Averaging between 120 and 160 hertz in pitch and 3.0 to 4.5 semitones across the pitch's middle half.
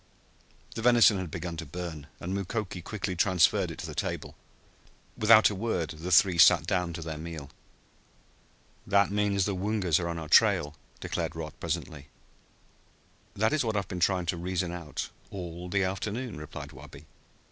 No: very low, 90 Hz; average, 3.3 semitones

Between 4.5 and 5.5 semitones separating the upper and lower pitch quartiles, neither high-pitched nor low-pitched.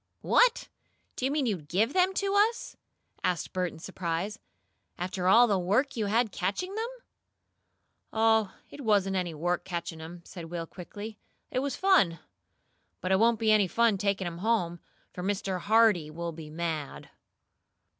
No: average, 4.8 semitones; high, 195 Hz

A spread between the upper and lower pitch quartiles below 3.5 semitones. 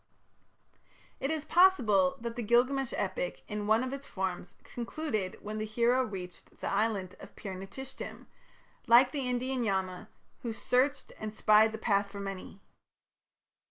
No: average, 4.4 semitones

